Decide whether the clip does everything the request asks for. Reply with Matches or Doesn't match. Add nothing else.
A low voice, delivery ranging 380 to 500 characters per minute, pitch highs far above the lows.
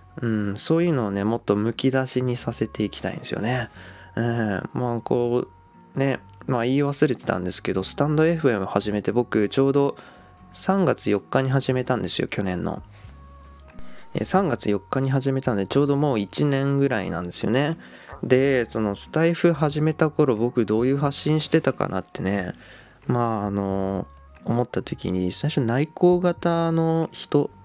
Doesn't match